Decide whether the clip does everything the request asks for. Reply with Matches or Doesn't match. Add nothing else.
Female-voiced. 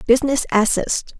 Matches